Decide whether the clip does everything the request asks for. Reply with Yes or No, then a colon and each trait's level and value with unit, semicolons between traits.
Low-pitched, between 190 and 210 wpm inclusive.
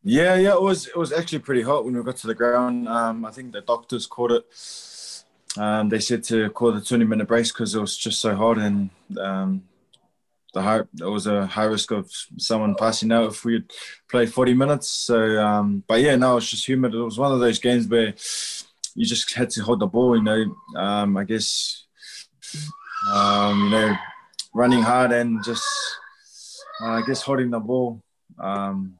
Yes: low, 115 Hz; average, 200 wpm